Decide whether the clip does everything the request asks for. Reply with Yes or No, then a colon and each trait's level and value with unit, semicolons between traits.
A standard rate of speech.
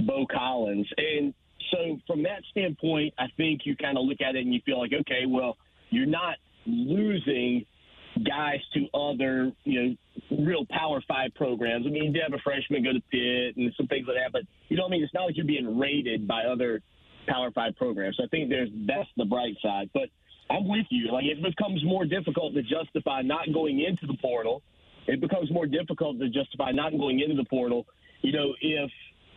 No: fast, 210 wpm